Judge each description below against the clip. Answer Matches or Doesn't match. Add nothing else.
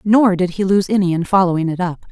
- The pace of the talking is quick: Matches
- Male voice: Doesn't match